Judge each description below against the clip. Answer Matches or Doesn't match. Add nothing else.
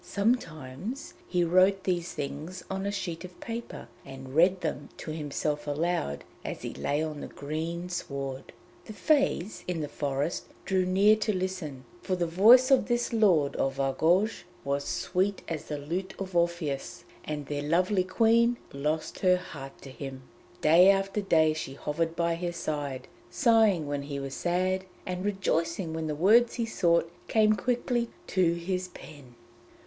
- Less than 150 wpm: Doesn't match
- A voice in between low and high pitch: Matches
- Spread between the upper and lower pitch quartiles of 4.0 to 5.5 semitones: Matches